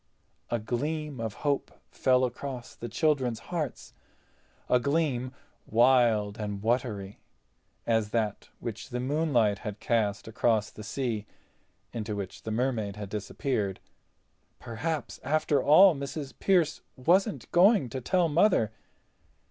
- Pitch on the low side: Yes, low, 125 Hz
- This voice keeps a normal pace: No, slow, 120 wpm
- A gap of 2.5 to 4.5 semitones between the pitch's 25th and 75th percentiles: No, average, 5.0 semitones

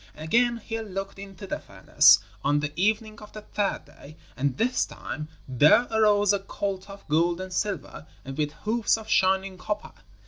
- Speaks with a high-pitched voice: Yes, high, 195 Hz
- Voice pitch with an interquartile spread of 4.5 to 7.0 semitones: Yes, average, 4.9 semitones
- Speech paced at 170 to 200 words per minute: Yes, average, 175 wpm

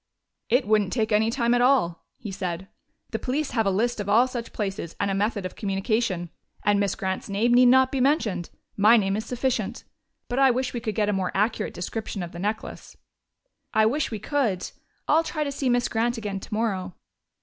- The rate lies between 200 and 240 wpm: Yes, fast, 205 wpm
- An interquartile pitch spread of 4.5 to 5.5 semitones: No, average, 3.8 semitones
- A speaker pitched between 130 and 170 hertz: No, high, 220 Hz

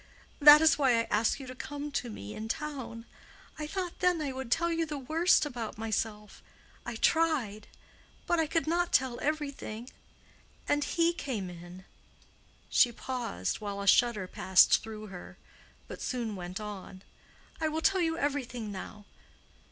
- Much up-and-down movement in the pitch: Yes, wide, 6.3 semitones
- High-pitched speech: Yes, very high, 250 Hz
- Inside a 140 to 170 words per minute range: Yes, average, 160 wpm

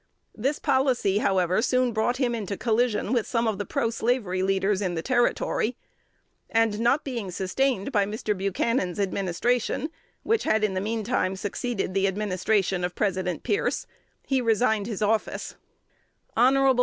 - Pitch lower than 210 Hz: No, high, 215 Hz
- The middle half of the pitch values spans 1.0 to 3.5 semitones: No, average, 4.1 semitones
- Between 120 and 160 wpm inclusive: Yes, average, 150 wpm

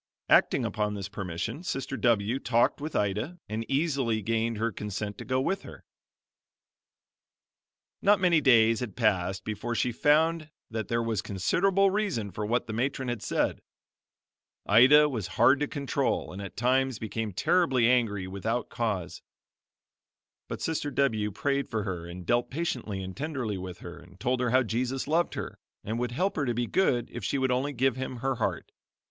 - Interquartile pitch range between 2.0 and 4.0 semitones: No, average, 4.6 semitones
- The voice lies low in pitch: Yes, low, 120 Hz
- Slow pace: No, average, 175 wpm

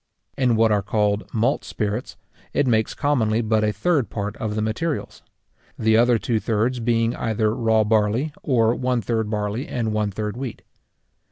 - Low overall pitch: Yes, low, 110 Hz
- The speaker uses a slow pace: No, average, 170 wpm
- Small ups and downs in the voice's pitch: Yes, narrow, 2.2 semitones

